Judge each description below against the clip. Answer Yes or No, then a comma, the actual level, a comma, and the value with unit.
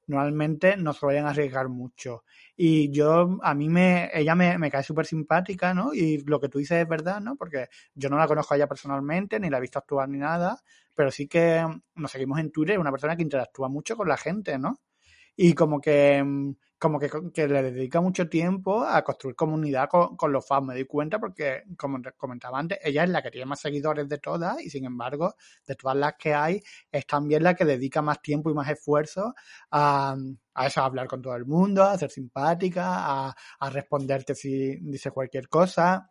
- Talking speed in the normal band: No, fast, 215 wpm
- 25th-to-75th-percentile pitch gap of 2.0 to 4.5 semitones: Yes, average, 3.4 semitones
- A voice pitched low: No, medium, 150 Hz